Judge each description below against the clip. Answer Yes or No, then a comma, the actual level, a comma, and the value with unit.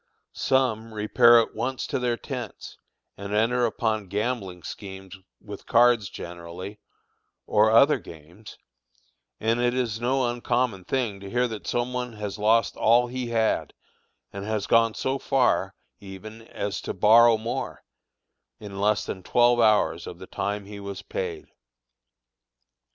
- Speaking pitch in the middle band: No, low, 110 Hz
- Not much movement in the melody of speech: No, average, 3.3 semitones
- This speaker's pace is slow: No, average, 145 wpm